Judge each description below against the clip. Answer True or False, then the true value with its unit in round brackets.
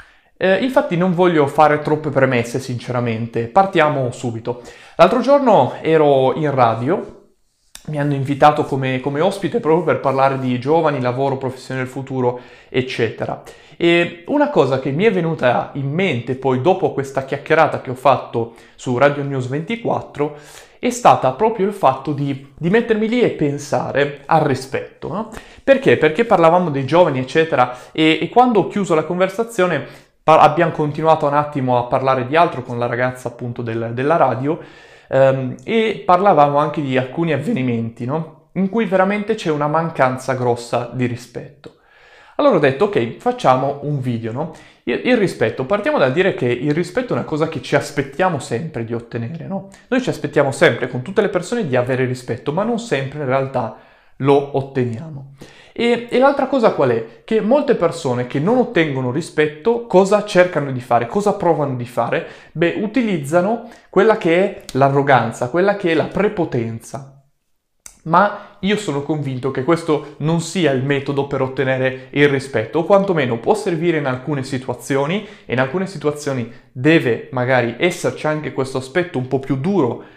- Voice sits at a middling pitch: True (150 Hz)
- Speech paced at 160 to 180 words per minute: True (165 wpm)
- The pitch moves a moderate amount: False (5.7 semitones)